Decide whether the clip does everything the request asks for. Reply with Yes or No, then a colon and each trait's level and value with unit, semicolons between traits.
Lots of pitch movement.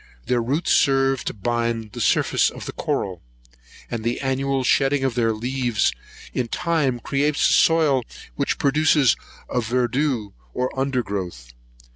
No: average, 3.0 semitones